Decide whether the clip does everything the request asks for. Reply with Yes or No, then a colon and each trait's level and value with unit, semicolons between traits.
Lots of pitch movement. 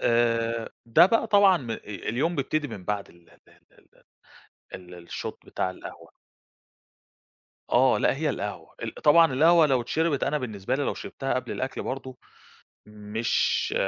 Yes: wide, 5.8 semitones